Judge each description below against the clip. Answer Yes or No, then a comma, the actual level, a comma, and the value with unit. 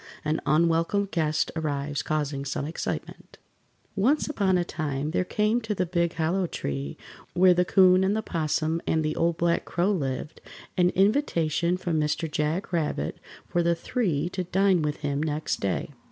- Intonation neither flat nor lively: Yes, average, 3.3 semitones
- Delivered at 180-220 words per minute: No, average, 170 wpm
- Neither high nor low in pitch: Yes, medium, 165 Hz